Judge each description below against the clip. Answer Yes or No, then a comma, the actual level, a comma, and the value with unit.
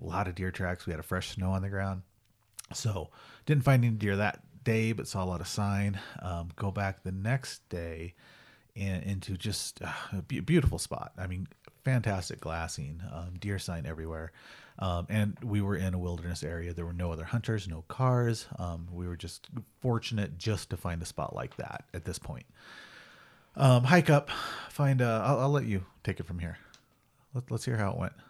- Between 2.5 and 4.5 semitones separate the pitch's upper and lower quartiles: No, average, 4.9 semitones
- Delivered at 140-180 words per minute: No, average, 200 wpm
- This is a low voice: Yes, low, 100 Hz